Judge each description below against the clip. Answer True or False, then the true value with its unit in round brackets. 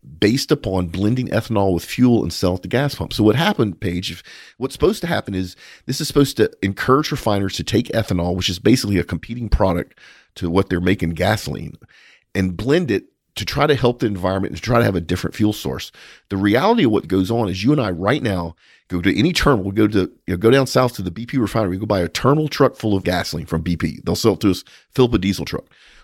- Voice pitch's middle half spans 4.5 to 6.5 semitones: True (4.8 semitones)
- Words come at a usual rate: False (250 wpm)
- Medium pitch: False (100 Hz)